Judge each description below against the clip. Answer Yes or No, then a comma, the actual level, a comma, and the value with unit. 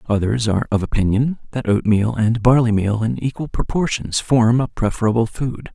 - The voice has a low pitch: Yes, low, 115 Hz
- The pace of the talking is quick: No, average, 155 wpm